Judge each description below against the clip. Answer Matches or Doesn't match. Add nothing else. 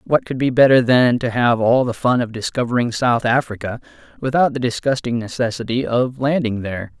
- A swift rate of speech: Doesn't match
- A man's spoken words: Matches